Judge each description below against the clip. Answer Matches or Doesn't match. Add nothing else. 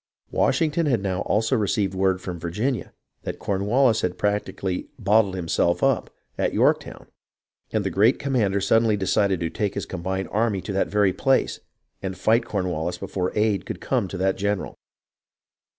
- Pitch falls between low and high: Doesn't match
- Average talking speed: Matches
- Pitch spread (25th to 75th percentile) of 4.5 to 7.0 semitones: Doesn't match